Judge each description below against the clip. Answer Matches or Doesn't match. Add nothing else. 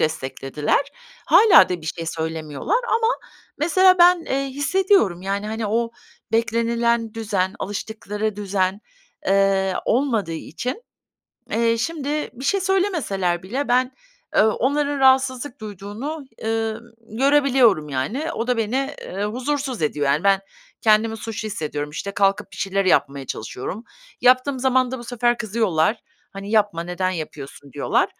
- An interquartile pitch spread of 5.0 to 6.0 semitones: Matches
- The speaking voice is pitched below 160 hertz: Doesn't match